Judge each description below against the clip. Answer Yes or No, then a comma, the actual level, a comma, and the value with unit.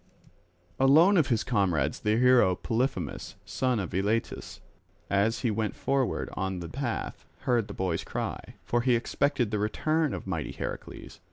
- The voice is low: Yes, low, 115 Hz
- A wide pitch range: No, average, 4.8 semitones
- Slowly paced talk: No, average, 155 wpm